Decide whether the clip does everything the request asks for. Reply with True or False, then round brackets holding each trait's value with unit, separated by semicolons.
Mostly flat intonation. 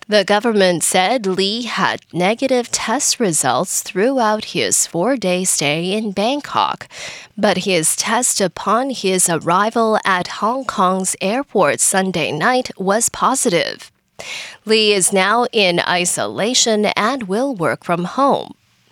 False (3.9 semitones)